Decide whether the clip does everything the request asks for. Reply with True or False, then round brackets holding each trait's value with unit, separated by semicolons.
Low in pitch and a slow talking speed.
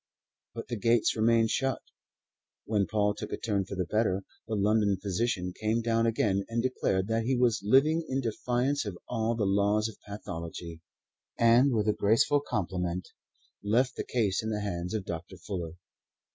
False (110 Hz; 175 wpm)